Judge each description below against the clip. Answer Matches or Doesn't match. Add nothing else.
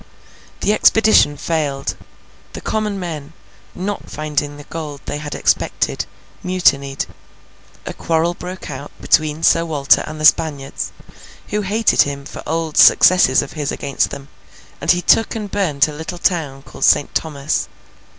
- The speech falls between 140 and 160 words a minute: Matches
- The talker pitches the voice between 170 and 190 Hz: Doesn't match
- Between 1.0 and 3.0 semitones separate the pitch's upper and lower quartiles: Doesn't match